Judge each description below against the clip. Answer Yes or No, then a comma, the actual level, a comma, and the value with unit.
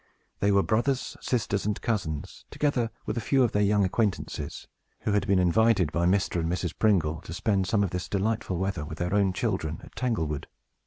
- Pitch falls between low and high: No, low, 100 Hz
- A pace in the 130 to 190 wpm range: No, average, 200 wpm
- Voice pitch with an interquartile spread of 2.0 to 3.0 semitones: No, average, 3.8 semitones